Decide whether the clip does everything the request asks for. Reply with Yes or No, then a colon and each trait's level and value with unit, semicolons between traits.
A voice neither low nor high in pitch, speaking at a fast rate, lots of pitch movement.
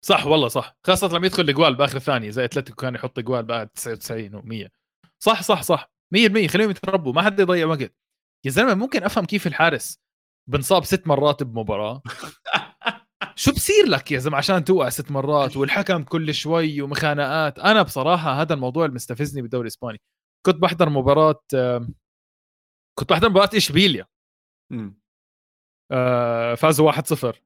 Yes: medium, 145 Hz; fast, 145 wpm; wide, 6.3 semitones